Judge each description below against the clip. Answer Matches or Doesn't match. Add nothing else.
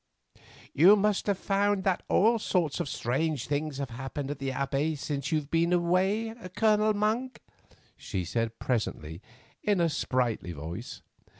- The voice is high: Doesn't match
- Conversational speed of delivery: Matches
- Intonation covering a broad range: Matches